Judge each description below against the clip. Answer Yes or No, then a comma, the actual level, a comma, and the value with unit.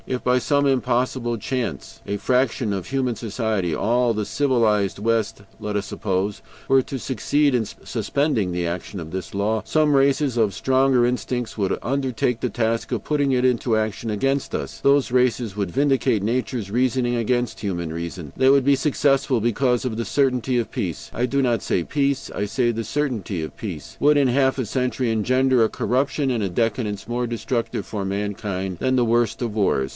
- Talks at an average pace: Yes, average, 185 wpm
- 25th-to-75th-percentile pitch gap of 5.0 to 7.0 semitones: No, average, 4.0 semitones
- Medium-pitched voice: No, low, 120 Hz